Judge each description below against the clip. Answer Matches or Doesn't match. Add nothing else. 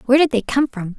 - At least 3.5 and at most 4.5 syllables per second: Doesn't match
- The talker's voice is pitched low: Doesn't match